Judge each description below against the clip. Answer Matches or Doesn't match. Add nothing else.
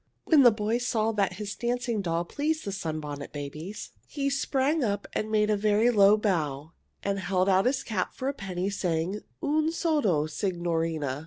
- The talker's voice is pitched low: Doesn't match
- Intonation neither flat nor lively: Doesn't match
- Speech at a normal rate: Matches